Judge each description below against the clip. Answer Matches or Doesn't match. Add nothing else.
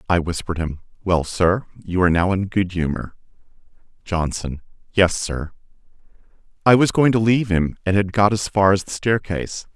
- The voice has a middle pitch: Doesn't match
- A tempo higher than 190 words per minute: Doesn't match